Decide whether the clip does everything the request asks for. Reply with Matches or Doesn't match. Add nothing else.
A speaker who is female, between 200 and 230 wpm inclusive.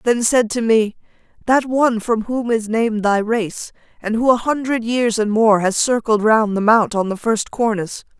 Matches